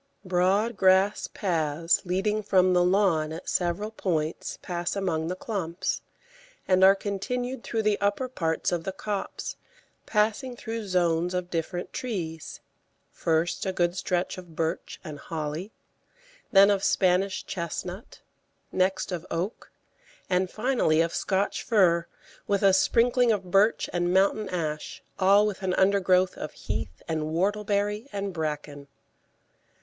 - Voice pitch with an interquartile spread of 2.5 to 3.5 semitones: Yes, average, 3.1 semitones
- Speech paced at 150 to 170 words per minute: No, slow, 135 wpm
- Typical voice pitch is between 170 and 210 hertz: Yes, medium, 185 Hz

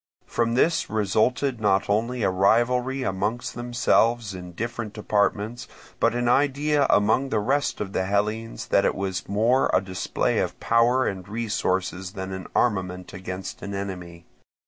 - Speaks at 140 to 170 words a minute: Yes, average, 155 wpm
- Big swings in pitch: No, average, 4.2 semitones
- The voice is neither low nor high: No, low, 105 Hz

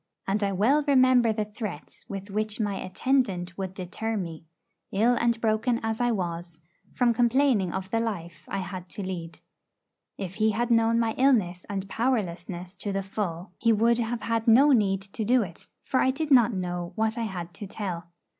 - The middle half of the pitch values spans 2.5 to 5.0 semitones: Yes, average, 4.0 semitones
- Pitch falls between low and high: No, high, 210 Hz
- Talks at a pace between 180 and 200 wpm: Yes, average, 190 wpm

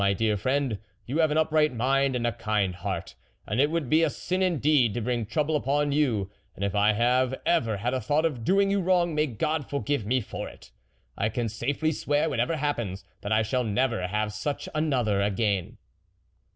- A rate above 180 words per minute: Yes, fast, 205 wpm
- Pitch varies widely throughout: Yes, wide, 5.8 semitones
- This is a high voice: No, low, 130 Hz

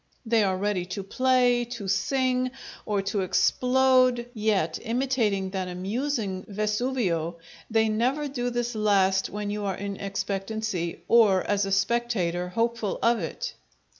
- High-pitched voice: Yes, high, 215 Hz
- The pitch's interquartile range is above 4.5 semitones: No, average, 3.8 semitones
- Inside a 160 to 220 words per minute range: No, slow, 135 wpm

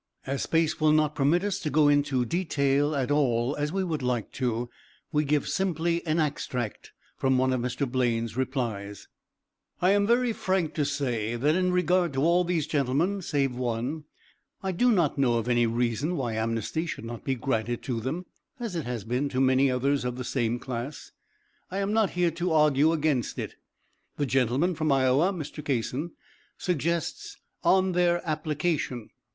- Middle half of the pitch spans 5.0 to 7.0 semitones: Yes, average, 5.3 semitones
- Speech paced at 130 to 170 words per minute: No, average, 180 wpm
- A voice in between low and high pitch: Yes, medium, 145 Hz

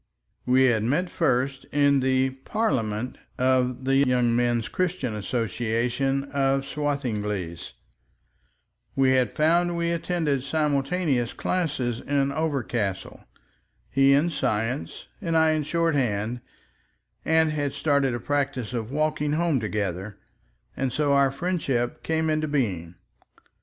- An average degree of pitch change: Yes, average, 4.0 semitones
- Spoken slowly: Yes, slow, 120 wpm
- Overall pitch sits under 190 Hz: Yes, low, 135 Hz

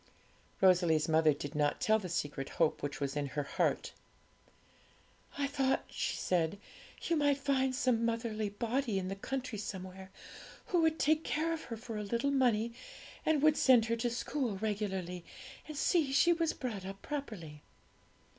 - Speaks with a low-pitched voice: No, high, 225 Hz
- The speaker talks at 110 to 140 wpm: No, average, 165 wpm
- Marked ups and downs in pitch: Yes, wide, 7.0 semitones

